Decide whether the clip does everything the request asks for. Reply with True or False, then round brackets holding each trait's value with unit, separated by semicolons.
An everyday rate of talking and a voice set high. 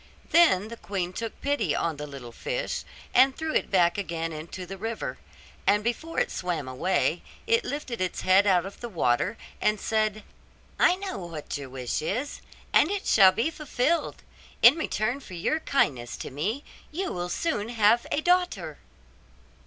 True (170 wpm; 210 Hz)